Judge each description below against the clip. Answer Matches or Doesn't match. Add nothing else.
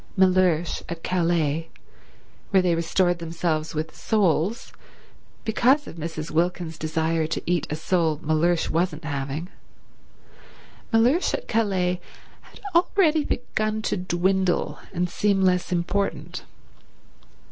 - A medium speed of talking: Doesn't match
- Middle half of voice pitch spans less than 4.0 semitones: Matches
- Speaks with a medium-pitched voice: Matches